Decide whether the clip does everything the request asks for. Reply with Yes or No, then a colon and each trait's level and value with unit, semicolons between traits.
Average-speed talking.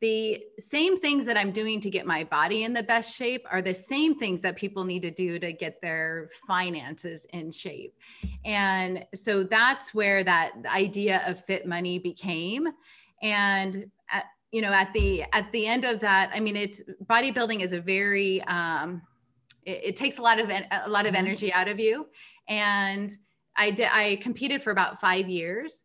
Yes: average, 185 wpm